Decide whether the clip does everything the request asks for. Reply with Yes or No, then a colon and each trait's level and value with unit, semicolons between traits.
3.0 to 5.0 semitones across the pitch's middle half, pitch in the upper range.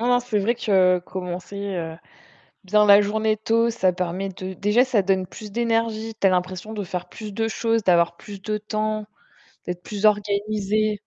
No: narrow, 2.6 semitones; high, 210 Hz